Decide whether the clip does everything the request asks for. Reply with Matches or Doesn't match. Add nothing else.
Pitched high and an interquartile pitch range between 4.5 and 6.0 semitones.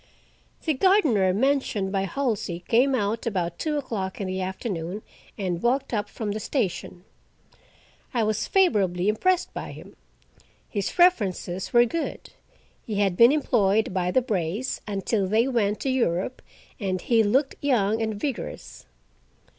Matches